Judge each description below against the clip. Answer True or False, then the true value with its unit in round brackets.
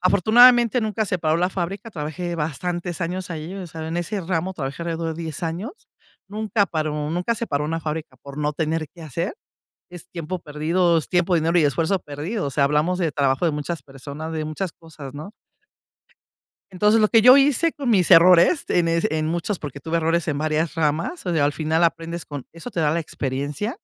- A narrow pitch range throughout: False (3.1 semitones)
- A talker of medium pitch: True (165 Hz)